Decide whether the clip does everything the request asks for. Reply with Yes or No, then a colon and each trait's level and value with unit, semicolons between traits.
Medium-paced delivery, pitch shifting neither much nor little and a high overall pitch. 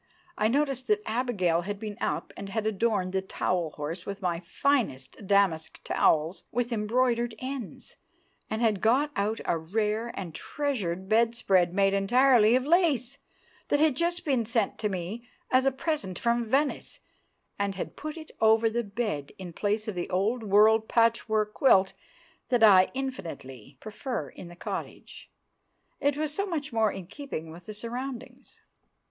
Yes: average, 160 wpm; average, 4.9 semitones; high, 220 Hz